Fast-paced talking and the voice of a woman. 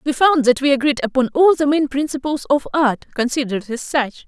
Yes: fast, 210 wpm; female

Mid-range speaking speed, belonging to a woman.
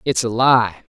No: average, 180 wpm; male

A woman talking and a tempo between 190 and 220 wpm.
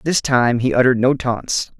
No: male; average, 200 wpm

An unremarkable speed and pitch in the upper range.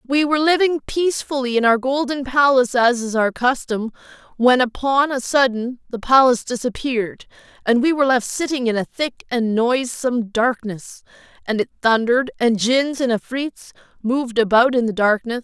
Yes: average, 165 wpm; very high, 250 Hz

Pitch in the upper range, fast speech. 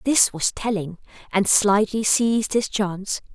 No: high, 210 Hz; average, 145 wpm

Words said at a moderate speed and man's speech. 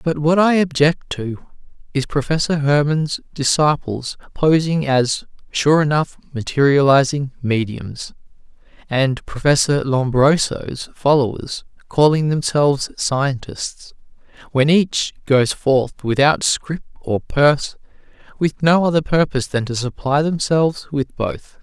No: slow, 110 wpm; male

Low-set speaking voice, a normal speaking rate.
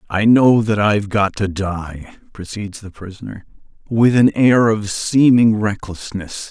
Yes: low, 105 Hz; average, 150 wpm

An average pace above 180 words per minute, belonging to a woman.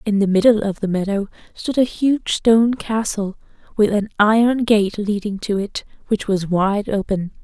No: average, 175 wpm; female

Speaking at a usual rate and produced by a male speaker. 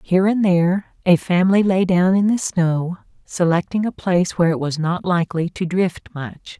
No: average, 190 wpm; female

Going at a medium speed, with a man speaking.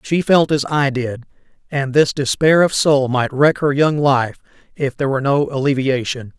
Yes: average, 190 wpm; male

